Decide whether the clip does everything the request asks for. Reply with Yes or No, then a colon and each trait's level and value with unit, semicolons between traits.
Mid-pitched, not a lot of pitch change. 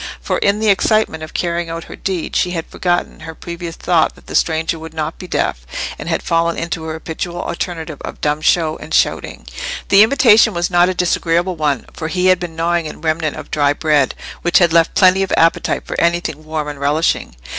Yes: medium, 165 Hz; narrow, 2.0 semitones